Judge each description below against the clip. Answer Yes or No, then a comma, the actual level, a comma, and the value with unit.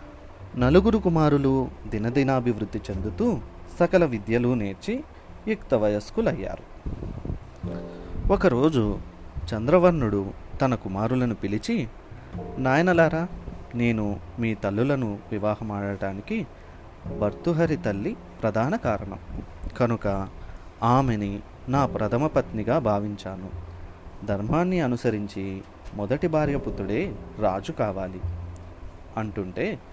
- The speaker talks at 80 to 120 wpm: No, slow, 70 wpm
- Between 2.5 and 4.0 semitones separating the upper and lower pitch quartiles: No, wide, 5.6 semitones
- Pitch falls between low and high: No, low, 105 Hz